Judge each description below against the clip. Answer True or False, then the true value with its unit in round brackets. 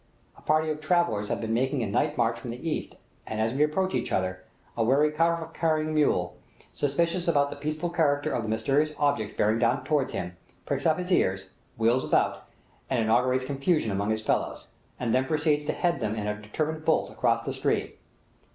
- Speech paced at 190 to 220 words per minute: True (200 wpm)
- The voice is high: False (140 Hz)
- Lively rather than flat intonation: True (5.7 semitones)